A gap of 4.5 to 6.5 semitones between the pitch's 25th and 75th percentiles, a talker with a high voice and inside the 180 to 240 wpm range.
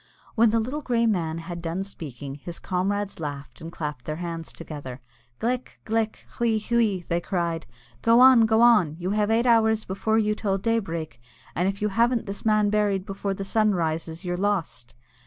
Yes: average, 5.0 semitones; high, 195 Hz; average, 190 wpm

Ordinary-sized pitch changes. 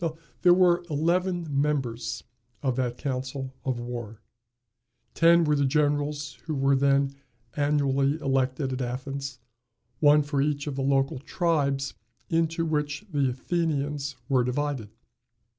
No: narrow, 2.2 semitones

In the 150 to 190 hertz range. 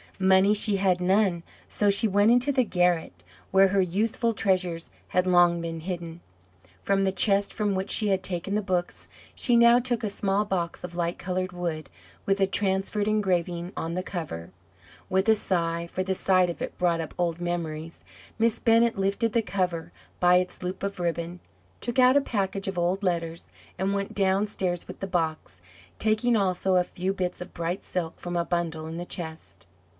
Yes: medium, 185 Hz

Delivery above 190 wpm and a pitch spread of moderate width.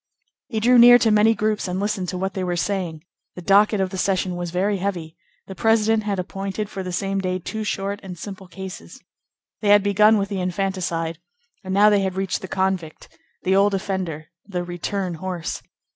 No: average, 200 wpm; narrow, 2.1 semitones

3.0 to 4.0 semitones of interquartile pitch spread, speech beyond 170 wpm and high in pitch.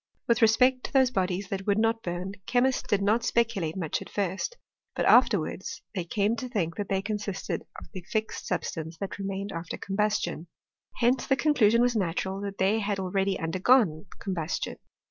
Yes: average, 3.7 semitones; average, 180 wpm; high, 200 Hz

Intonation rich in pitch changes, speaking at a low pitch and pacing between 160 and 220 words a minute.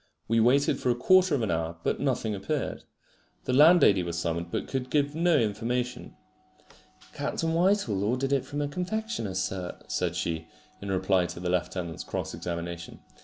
Yes: wide, 8.1 semitones; low, 115 Hz; average, 170 wpm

